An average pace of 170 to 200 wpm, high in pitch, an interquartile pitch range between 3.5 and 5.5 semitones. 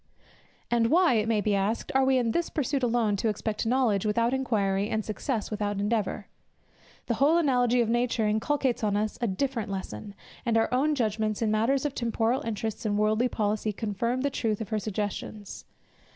No: average, 185 wpm; high, 225 Hz; average, 2.9 semitones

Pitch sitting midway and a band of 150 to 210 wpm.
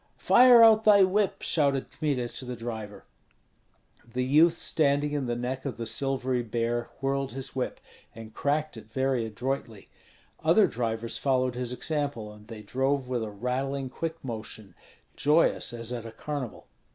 No: low, 130 Hz; average, 160 wpm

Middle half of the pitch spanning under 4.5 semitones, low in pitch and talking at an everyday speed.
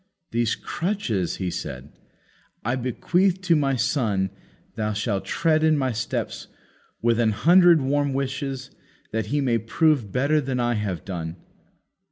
No: wide, 5.5 semitones; low, 125 Hz; average, 145 wpm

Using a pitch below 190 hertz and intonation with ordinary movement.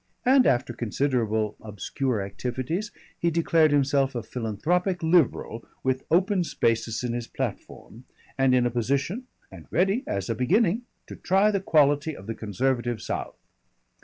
No: low, 135 Hz; wide, 6.6 semitones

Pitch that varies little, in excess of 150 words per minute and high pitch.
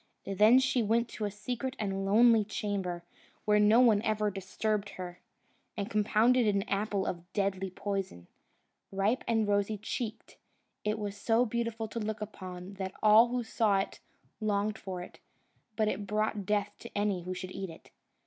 Yes: narrow, 2.1 semitones; average, 170 wpm; high, 210 Hz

